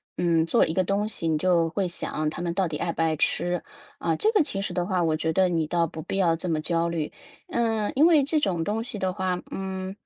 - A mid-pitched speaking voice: Yes, medium, 180 Hz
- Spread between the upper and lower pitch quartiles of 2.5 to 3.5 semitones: Yes, average, 3.1 semitones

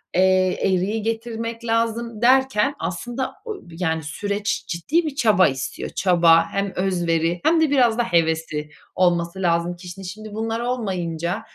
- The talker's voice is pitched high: Yes, high, 195 Hz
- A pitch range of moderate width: Yes, average, 5.0 semitones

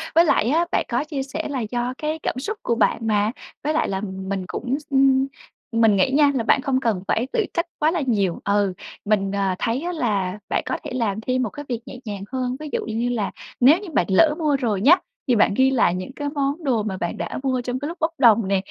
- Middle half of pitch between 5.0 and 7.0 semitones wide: Yes, wide, 5.6 semitones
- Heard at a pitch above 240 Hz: Yes, very high, 250 Hz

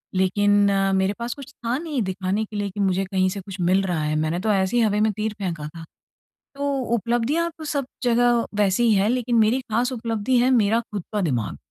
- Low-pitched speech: No, high, 210 Hz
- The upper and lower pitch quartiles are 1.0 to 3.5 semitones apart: No, average, 4.1 semitones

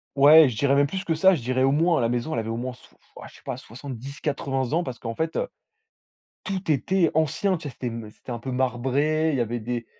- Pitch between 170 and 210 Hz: No, low, 135 Hz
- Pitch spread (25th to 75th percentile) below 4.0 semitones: No, average, 4.7 semitones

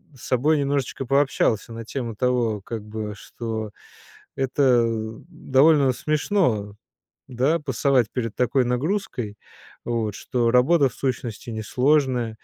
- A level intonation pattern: No, average, 3.5 semitones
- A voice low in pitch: Yes, low, 125 Hz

